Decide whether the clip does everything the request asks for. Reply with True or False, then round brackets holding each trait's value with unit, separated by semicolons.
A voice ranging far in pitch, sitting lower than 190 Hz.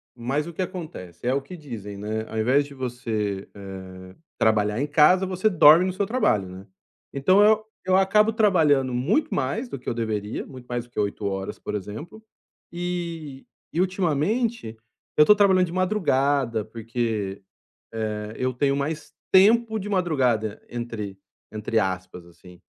True (9.0 semitones; 135 Hz)